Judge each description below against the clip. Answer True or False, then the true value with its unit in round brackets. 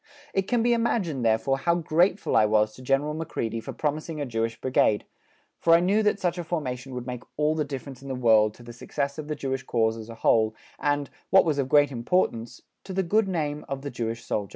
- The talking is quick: True (230 wpm)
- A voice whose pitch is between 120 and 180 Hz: True (140 Hz)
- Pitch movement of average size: False (5.8 semitones)